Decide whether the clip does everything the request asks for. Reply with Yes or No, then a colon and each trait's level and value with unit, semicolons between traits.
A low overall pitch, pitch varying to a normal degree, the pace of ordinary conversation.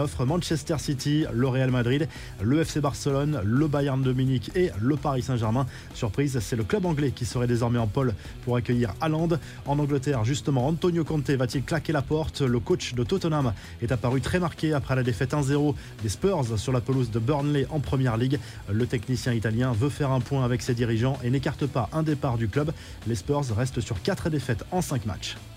Yes: low, 130 Hz; average, 3.2 semitones; average, 200 wpm